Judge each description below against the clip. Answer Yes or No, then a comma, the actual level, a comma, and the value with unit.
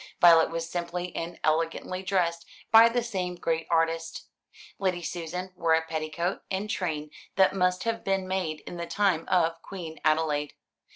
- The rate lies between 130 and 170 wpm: Yes, average, 160 wpm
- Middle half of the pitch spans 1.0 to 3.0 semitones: Yes, narrow, 2.4 semitones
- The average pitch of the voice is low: No, medium, 170 Hz